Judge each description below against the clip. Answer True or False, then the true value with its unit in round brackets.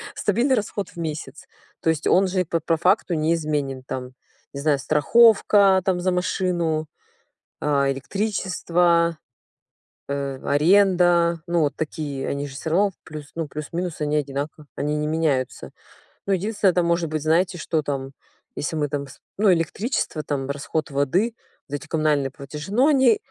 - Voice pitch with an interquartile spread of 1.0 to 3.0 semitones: False (4.0 semitones)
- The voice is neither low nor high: True (160 Hz)